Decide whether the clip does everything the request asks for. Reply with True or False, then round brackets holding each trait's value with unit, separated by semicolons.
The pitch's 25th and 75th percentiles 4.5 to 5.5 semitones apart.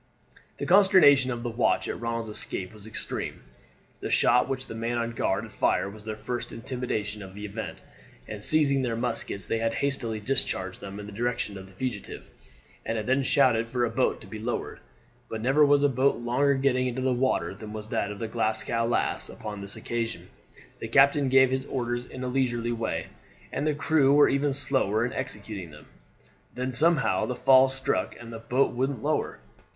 False (3.4 semitones)